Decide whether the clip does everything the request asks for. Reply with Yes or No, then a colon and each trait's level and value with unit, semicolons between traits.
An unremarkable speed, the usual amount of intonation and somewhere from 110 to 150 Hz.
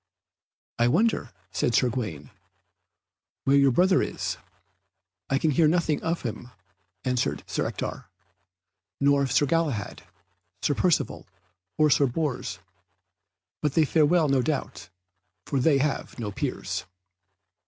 No: slow, 130 wpm; average, 4.1 semitones; medium, 140 Hz